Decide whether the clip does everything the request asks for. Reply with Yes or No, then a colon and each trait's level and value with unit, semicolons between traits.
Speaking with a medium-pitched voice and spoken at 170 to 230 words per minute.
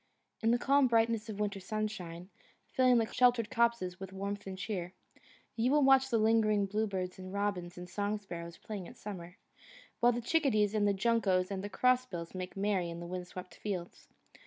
No: high, 205 Hz; average, 185 wpm